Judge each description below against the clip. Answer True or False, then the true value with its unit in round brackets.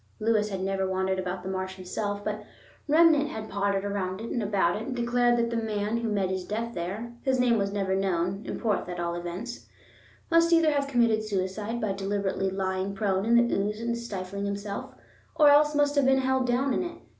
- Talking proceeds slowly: False (205 wpm)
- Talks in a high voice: True (210 Hz)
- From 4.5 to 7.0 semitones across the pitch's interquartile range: False (3.8 semitones)